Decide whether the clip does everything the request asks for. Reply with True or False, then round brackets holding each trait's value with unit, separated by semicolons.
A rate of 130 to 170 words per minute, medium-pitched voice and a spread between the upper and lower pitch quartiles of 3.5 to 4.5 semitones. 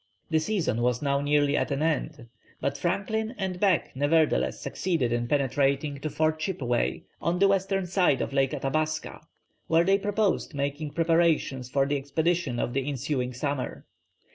True (160 wpm; 150 Hz; 3.9 semitones)